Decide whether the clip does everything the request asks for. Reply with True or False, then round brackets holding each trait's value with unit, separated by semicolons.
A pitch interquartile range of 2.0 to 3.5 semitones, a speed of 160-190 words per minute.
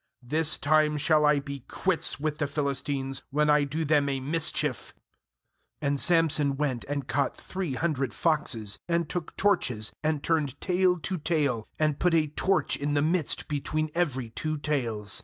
True (2.4 semitones; 170 wpm)